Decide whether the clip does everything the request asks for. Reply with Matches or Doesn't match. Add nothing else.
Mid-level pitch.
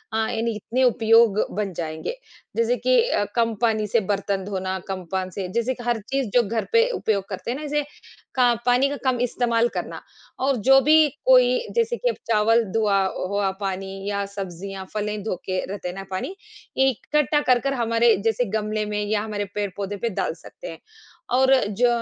Doesn't match